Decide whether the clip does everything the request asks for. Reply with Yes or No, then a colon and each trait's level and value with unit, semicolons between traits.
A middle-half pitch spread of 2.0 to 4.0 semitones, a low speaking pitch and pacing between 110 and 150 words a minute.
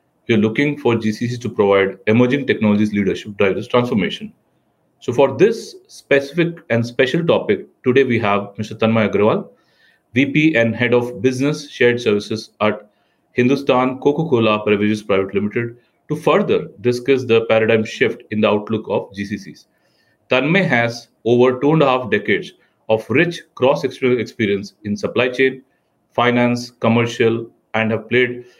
Yes: average, 3.0 semitones; low, 120 Hz; average, 145 wpm